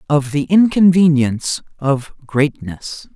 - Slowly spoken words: Yes, slow, 95 wpm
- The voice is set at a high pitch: No, medium, 150 Hz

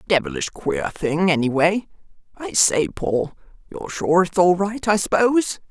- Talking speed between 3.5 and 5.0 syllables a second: Yes, 4.6 syllables/s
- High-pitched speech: No, medium, 175 Hz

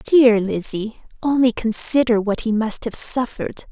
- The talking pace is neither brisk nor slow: Yes, average, 145 wpm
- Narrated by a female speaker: Yes, female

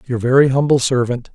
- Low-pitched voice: Yes, low, 130 Hz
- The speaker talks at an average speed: Yes, average, 180 wpm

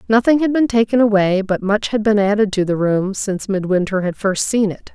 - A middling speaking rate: No, fast, 230 wpm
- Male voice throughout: No, female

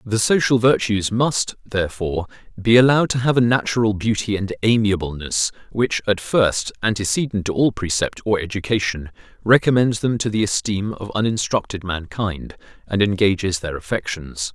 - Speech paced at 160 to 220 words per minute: No, average, 145 wpm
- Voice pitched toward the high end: No, low, 105 Hz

